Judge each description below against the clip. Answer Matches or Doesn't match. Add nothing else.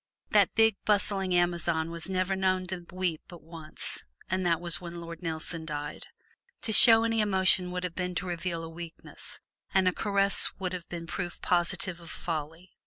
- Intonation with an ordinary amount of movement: Doesn't match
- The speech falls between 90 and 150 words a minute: Doesn't match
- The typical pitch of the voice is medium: Matches